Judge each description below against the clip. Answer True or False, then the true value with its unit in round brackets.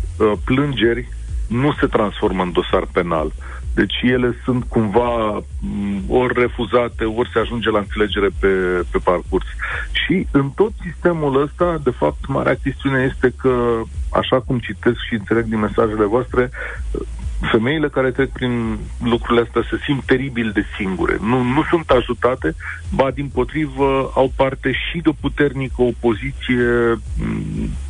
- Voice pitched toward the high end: False (120 Hz)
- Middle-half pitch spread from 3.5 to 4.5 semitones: True (4.0 semitones)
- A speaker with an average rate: True (140 wpm)